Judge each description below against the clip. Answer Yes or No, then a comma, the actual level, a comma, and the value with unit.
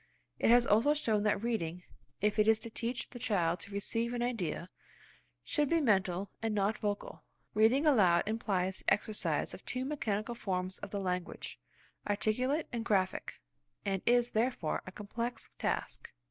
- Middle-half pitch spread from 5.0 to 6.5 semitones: No, average, 3.9 semitones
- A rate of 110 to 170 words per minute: Yes, average, 155 wpm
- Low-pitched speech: No, high, 215 Hz